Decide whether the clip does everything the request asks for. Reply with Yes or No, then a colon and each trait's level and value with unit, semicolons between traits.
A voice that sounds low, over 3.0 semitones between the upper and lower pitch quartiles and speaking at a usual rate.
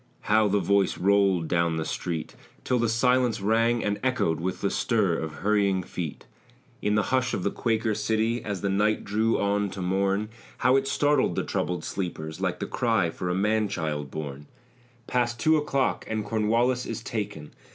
Yes: low, 105 Hz; average, 3.8 semitones; average, 185 wpm